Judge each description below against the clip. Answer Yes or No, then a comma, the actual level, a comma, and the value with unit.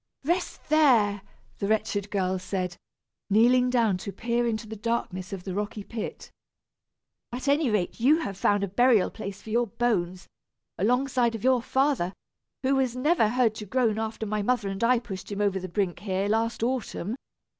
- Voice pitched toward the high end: Yes, high, 220 Hz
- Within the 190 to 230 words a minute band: No, average, 175 wpm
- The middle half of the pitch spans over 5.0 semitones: No, average, 3.8 semitones